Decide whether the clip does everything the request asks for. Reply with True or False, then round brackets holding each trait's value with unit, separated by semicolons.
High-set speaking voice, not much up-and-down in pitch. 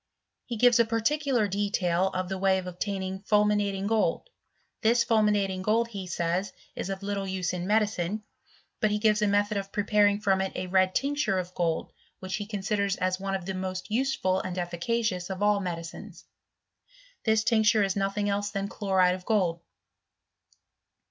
True (200 Hz; 2.3 semitones)